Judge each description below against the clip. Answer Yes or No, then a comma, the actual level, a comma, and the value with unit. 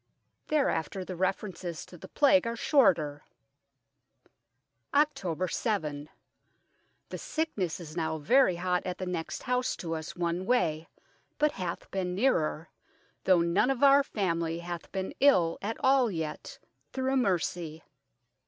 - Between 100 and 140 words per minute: Yes, slow, 135 wpm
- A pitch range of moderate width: No, wide, 6.6 semitones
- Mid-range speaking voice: Yes, medium, 180 Hz